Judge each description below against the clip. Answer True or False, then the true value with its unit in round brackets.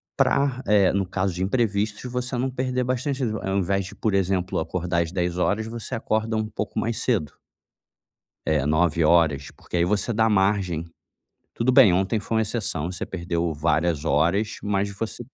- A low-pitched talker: True (100 Hz)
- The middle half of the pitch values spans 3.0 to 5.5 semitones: True (4.3 semitones)